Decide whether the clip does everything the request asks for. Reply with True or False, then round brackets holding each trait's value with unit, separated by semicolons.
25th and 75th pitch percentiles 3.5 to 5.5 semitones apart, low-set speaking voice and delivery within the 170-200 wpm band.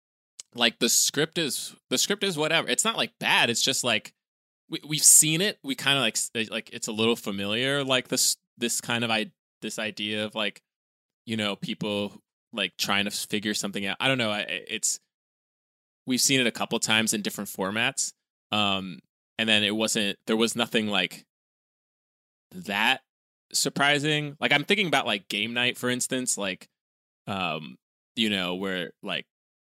True (4.4 semitones; 115 Hz; 175 wpm)